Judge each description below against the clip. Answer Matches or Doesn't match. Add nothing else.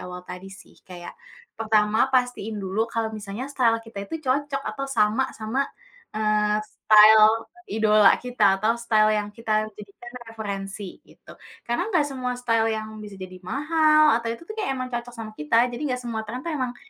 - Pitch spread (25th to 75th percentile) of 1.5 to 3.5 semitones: Matches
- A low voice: Doesn't match